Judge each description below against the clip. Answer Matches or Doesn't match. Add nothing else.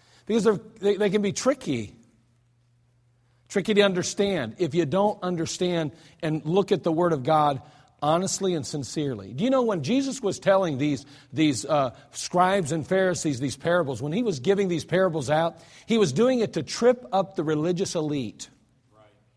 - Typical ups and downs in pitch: Doesn't match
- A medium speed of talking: Matches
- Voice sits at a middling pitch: Matches